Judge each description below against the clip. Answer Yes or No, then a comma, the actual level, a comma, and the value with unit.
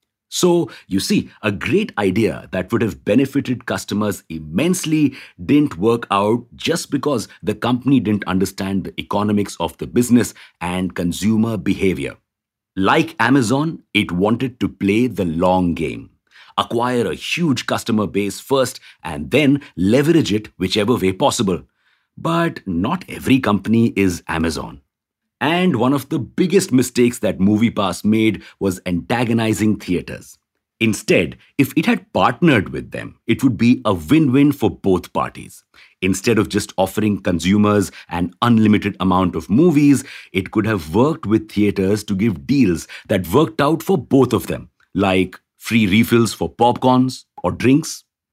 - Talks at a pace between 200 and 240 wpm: No, average, 145 wpm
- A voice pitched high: No, low, 110 Hz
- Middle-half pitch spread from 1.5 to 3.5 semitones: No, average, 5.1 semitones